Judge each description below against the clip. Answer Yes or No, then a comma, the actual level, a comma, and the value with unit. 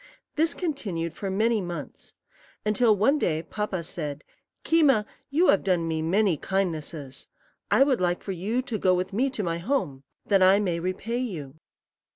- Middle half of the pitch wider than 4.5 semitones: Yes, wide, 5.5 semitones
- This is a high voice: Yes, high, 195 Hz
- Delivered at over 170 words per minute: No, average, 165 wpm